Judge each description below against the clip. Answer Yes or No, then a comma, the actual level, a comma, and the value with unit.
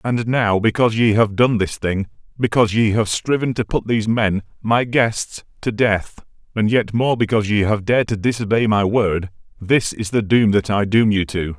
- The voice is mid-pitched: No, low, 110 Hz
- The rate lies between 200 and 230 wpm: Yes, fast, 205 wpm